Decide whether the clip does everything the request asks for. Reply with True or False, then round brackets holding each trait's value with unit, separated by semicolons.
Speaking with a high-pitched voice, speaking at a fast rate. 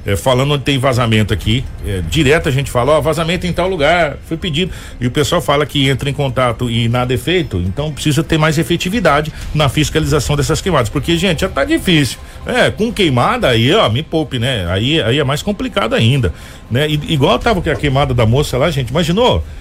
False (145 Hz; 215 wpm)